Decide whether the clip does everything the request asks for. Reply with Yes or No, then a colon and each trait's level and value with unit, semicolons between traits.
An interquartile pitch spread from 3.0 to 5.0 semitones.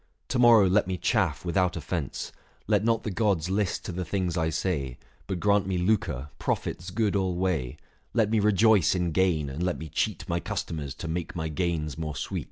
Yes: average, 3.8 semitones